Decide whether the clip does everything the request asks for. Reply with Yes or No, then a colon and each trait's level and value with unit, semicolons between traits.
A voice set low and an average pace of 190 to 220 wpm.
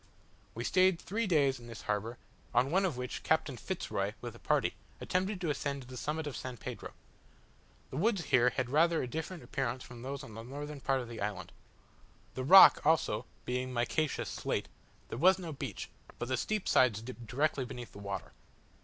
Yes: low, 130 Hz; average, 200 wpm